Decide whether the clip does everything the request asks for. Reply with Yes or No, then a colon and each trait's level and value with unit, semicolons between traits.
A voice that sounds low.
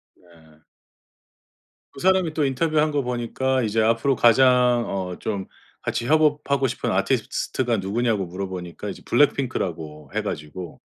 Yes: low, 120 Hz